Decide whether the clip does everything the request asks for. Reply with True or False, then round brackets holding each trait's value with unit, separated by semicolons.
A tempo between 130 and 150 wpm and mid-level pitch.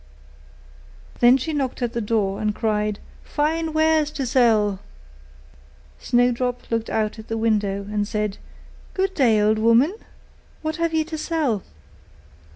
False (140 wpm; 235 Hz)